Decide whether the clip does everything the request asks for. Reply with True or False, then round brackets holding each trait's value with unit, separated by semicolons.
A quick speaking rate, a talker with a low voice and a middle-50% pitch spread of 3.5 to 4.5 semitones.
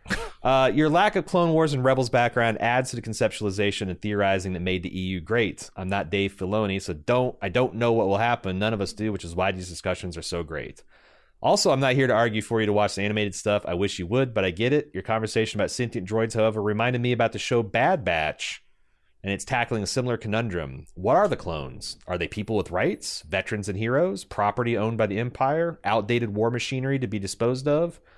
True (230 wpm; 110 Hz; 3.8 semitones)